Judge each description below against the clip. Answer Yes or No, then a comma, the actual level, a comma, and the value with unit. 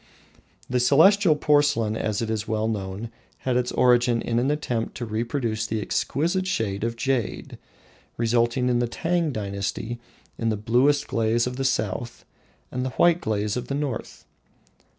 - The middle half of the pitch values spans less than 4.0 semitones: Yes, average, 3.5 semitones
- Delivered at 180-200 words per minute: No, average, 155 wpm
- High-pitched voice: No, low, 120 Hz